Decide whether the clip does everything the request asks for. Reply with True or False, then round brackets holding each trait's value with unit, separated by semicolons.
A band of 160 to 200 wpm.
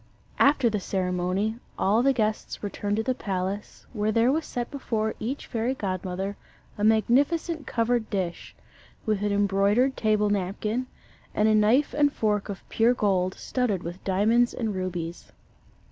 False (150 wpm)